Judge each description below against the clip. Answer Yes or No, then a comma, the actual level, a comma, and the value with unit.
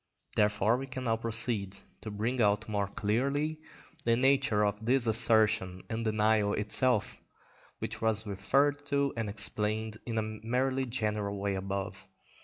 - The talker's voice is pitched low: Yes, low, 110 Hz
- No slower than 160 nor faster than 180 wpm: No, average, 145 wpm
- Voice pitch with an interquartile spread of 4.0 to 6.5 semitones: No, average, 3.1 semitones